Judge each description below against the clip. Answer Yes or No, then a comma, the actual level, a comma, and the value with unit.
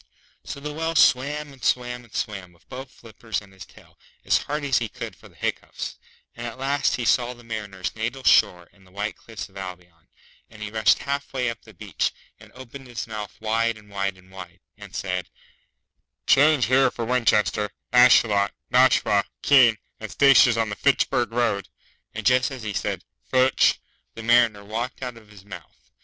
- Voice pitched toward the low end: Yes, low, 115 Hz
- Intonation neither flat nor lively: Yes, average, 3.9 semitones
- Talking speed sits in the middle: Yes, average, 190 wpm